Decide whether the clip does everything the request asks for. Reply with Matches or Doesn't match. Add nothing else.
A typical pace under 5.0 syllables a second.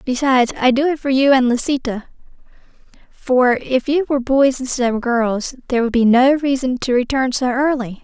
Doesn't match